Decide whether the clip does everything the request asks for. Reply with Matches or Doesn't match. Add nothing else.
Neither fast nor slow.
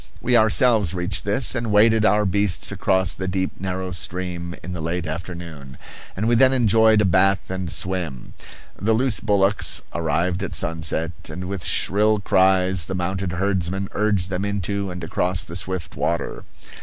Matches